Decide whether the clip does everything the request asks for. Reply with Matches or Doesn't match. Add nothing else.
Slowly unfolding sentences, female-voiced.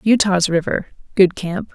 Matches